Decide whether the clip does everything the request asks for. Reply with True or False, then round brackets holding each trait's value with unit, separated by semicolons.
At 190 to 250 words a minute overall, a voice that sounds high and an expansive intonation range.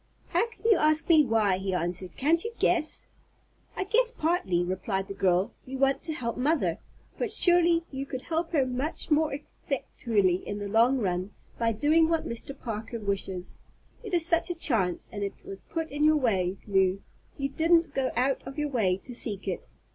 True (195 wpm; 260 Hz; 8.2 semitones)